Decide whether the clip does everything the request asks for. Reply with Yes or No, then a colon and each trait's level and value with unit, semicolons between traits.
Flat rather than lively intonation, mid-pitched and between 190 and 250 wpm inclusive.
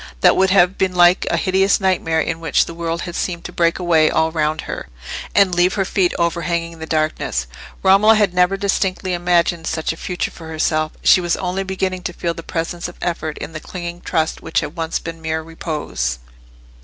Yes: narrow, 2.2 semitones; medium, 170 Hz; fast, 205 wpm